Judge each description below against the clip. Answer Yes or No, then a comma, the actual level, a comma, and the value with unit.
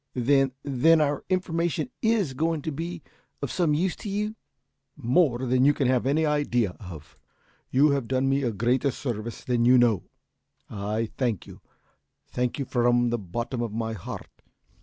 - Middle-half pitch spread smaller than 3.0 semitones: No, average, 4.2 semitones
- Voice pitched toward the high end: No, low, 130 Hz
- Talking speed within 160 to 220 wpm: Yes, average, 170 wpm